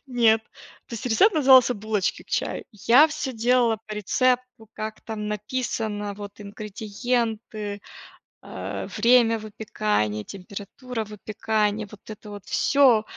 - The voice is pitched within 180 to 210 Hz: No, high, 220 Hz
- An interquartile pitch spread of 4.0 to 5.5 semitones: No, average, 2.9 semitones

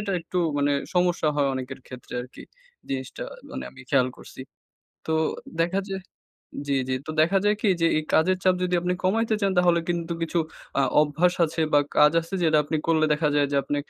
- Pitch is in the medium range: Yes, medium, 165 Hz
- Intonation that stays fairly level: No, average, 3.8 semitones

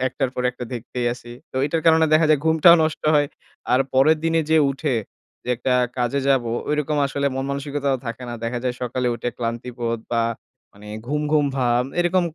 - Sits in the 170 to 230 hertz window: No, low, 135 Hz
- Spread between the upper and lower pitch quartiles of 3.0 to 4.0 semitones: Yes, average, 3.6 semitones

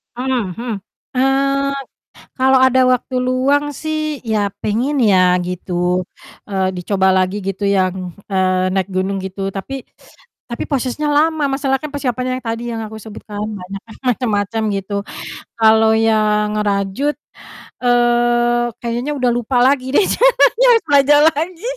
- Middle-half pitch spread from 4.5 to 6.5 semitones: Yes, average, 5.2 semitones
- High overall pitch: Yes, high, 235 Hz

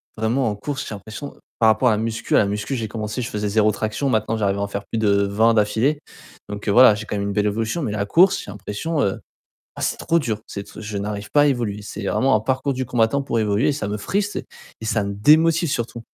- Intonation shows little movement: No, average, 4.0 semitones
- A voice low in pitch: Yes, low, 110 Hz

